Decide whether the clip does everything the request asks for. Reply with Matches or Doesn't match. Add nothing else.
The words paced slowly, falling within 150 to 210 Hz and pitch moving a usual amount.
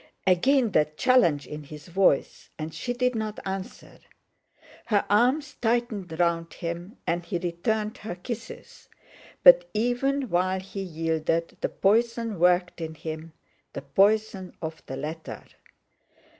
Doesn't match